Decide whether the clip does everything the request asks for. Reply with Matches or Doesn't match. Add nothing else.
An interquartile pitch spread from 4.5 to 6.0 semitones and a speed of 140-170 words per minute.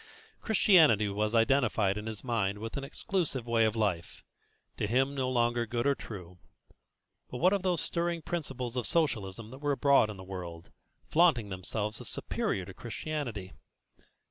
Matches